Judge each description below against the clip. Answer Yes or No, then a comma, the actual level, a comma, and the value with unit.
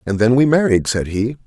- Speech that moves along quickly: Yes, fast, 245 wpm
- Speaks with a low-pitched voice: Yes, low, 120 Hz